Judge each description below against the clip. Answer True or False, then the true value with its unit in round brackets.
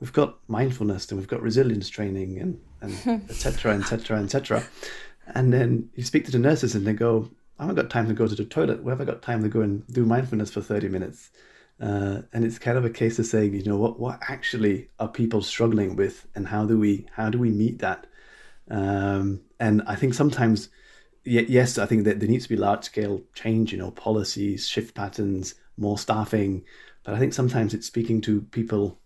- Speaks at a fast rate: True (210 wpm)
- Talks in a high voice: False (110 Hz)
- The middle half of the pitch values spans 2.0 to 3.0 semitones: True (2.5 semitones)